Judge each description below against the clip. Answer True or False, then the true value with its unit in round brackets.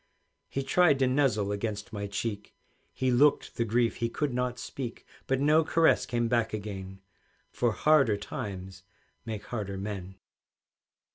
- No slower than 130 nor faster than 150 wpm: True (145 wpm)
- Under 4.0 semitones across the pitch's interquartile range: False (4.4 semitones)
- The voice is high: False (115 Hz)